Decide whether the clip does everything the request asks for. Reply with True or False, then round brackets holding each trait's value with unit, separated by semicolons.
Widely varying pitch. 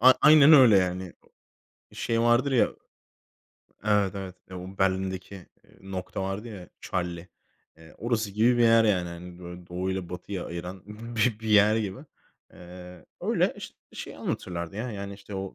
False (3.4 semitones)